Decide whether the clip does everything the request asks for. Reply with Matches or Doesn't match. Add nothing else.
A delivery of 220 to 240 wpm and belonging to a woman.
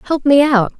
Matches